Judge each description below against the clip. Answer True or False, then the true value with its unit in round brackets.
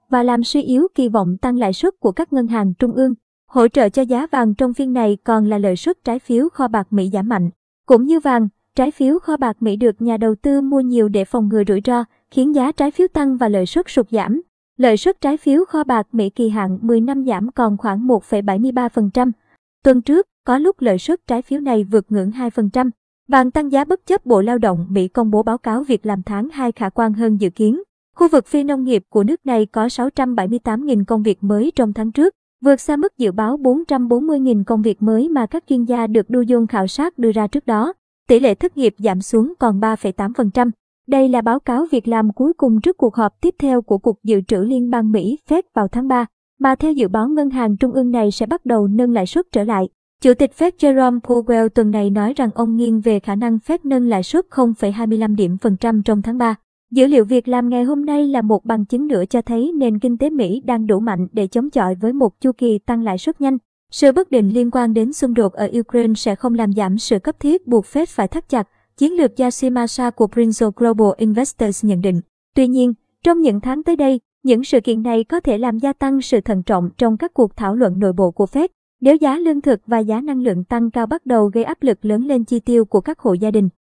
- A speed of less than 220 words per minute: False (245 wpm)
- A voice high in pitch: True (240 Hz)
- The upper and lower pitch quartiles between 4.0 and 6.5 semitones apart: False (3.4 semitones)